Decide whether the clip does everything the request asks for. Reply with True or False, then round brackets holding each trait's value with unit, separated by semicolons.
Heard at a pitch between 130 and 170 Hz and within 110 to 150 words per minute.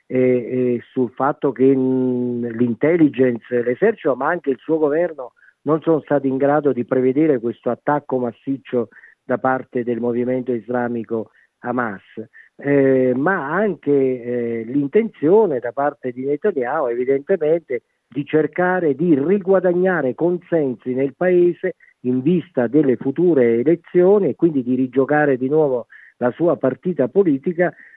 True (135 Hz; 130 wpm)